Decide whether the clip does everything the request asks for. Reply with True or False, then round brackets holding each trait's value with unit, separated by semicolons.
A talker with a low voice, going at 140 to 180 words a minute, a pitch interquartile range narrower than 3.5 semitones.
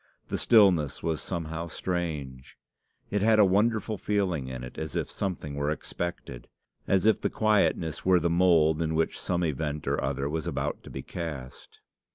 False (85 Hz; 175 wpm; 3.8 semitones)